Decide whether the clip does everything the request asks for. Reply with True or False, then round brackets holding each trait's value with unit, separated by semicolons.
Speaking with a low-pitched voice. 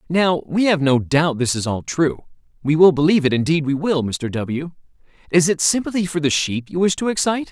False (160 Hz)